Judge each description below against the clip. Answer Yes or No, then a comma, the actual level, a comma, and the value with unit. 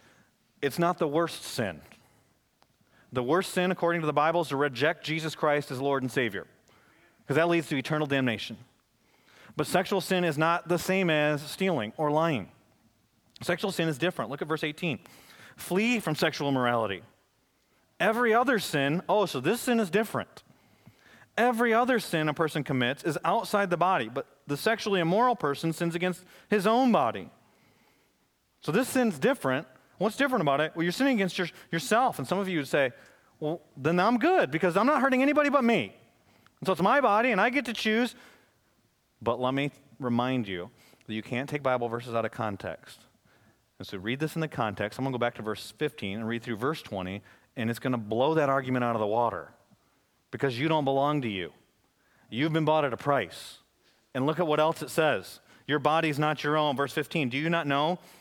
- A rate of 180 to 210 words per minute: Yes, average, 200 wpm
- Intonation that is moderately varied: No, wide, 6.1 semitones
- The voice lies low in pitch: No, medium, 155 Hz